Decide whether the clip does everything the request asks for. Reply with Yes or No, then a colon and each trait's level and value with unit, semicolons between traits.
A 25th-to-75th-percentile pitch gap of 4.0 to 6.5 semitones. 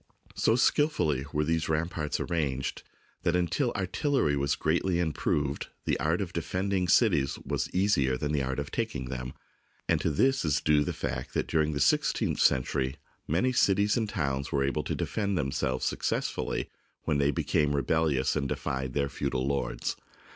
Yes: average, 4.5 semitones